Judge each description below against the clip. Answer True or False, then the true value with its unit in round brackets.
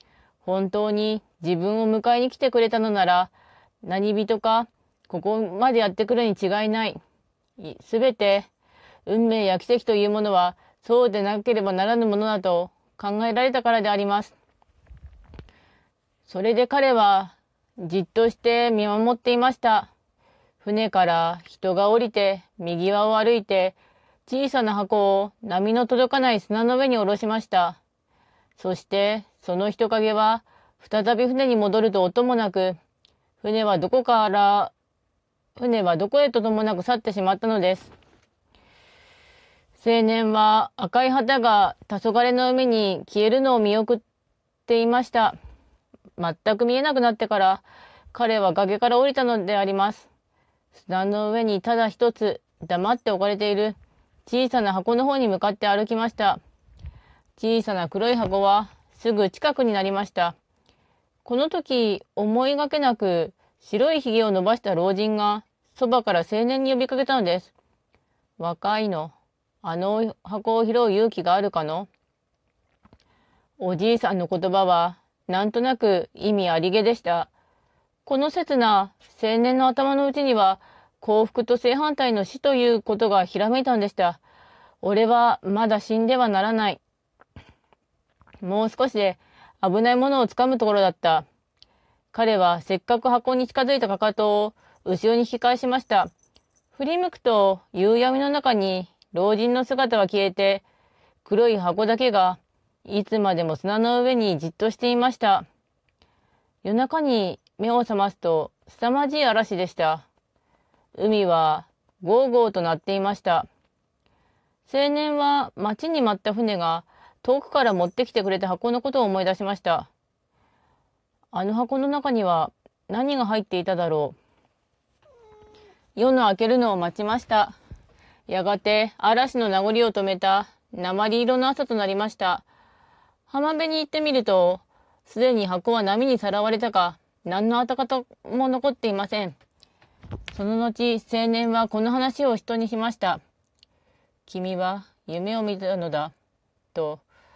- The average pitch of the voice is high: True (215 Hz)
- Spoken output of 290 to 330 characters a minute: False (270 characters per minute)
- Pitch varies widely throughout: False (3.9 semitones)